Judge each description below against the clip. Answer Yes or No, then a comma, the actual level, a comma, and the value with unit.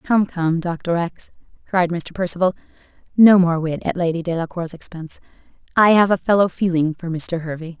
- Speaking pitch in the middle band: Yes, medium, 175 Hz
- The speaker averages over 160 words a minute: Yes, average, 170 wpm